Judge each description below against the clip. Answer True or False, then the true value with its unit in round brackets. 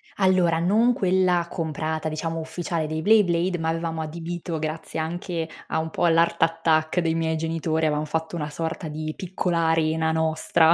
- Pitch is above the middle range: False (165 Hz)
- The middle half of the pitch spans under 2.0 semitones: True (1.3 semitones)